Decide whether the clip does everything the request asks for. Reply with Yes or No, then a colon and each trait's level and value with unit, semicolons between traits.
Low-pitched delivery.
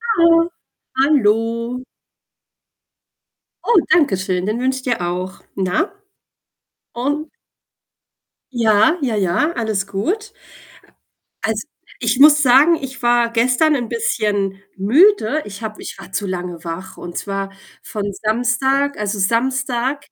No: high, 235 Hz